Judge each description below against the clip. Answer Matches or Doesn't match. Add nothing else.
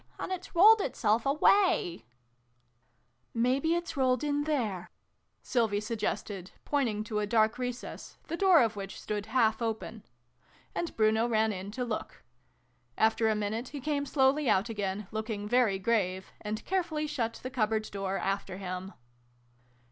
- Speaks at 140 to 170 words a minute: Matches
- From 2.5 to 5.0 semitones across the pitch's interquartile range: Matches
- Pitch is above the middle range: Matches